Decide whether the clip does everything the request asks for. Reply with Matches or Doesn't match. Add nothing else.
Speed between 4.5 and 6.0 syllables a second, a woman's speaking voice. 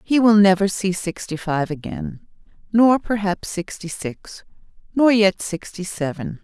Doesn't match